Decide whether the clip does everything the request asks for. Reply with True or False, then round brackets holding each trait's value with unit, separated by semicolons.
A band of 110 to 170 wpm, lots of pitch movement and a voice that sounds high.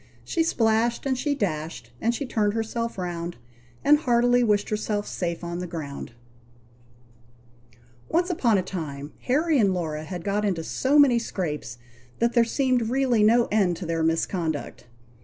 True (160 wpm; 6.2 semitones; 210 Hz)